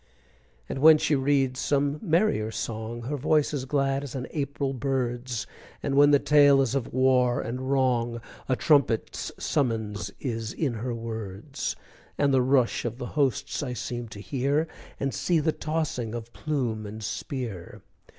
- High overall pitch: No, low, 130 Hz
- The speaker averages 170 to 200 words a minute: No, average, 160 wpm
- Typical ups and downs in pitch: Yes, average, 3.4 semitones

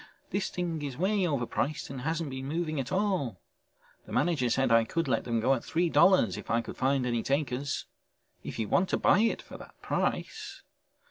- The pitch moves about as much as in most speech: No, wide, 5.8 semitones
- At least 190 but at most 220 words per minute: Yes, average, 200 wpm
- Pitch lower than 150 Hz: Yes, medium, 140 Hz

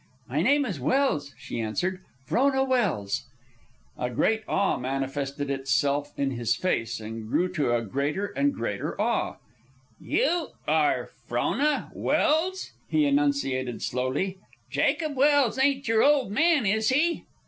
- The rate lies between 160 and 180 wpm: No, slow, 135 wpm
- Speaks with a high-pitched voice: Yes, high, 195 Hz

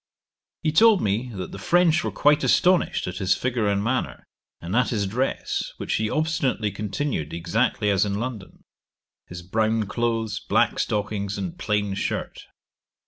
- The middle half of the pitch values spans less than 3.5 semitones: No, average, 4.5 semitones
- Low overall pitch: Yes, low, 110 Hz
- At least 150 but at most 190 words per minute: Yes, average, 155 wpm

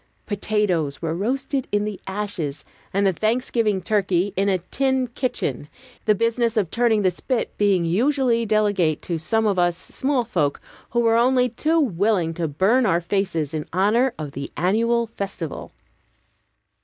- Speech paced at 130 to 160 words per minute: Yes, average, 155 wpm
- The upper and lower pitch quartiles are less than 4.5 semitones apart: No, average, 5.0 semitones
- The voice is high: Yes, high, 205 Hz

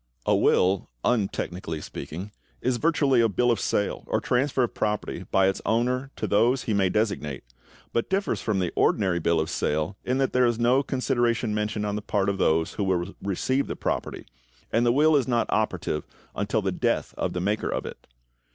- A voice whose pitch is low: Yes, low, 110 Hz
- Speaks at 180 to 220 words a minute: Yes, average, 200 wpm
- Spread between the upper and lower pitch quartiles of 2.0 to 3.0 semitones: No, average, 4.4 semitones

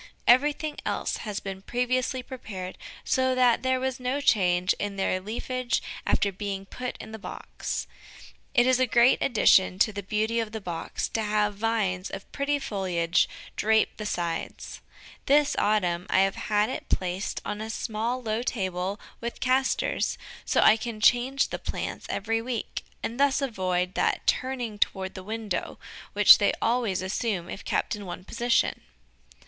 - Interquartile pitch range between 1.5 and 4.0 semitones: No, average, 4.5 semitones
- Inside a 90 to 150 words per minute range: No, average, 165 wpm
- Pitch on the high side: Yes, high, 220 Hz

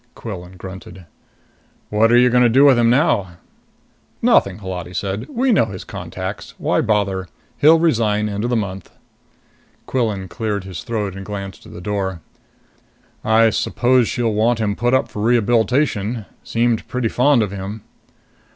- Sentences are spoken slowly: No, average, 160 wpm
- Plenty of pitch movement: No, average, 3.8 semitones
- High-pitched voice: No, low, 110 Hz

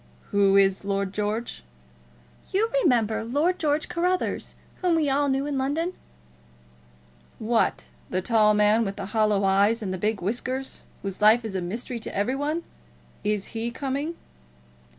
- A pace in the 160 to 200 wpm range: No, average, 150 wpm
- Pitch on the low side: No, high, 225 Hz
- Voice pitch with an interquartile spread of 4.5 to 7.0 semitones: Yes, wide, 5.6 semitones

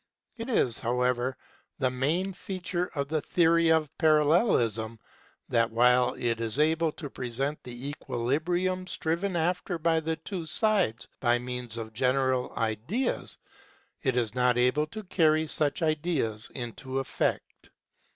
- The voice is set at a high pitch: No, medium, 140 Hz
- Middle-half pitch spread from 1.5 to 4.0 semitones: No, average, 5.3 semitones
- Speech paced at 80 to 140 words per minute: Yes, slow, 135 wpm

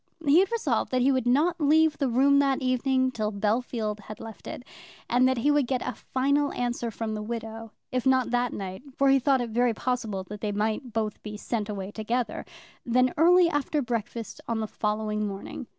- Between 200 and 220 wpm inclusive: Yes, fast, 205 wpm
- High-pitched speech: Yes, high, 245 Hz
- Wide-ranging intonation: No, average, 3.7 semitones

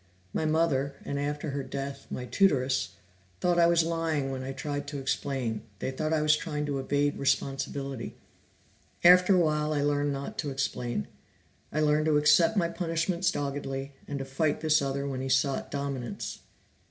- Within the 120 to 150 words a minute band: No, average, 175 wpm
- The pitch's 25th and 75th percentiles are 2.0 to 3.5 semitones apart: Yes, narrow, 2.4 semitones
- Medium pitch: Yes, medium, 145 Hz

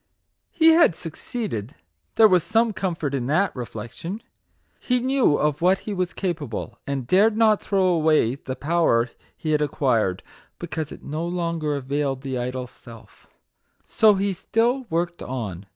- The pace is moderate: Yes, average, 150 wpm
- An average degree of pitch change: No, wide, 6.9 semitones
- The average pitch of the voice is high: No, medium, 160 Hz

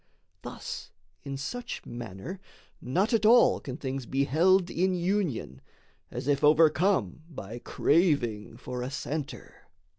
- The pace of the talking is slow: Yes, slow, 125 wpm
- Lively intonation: Yes, wide, 6.6 semitones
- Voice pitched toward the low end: No, medium, 150 Hz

